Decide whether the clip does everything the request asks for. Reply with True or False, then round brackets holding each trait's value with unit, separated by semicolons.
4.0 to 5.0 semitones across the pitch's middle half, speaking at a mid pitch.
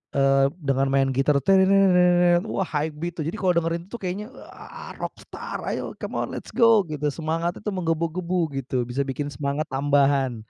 True (4.4 semitones; 160 Hz)